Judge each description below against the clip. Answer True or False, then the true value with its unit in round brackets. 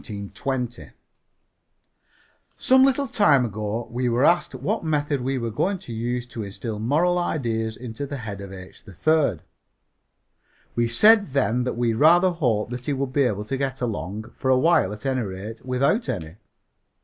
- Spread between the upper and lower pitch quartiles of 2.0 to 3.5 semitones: False (4.8 semitones)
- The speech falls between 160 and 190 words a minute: True (165 wpm)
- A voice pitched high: False (125 Hz)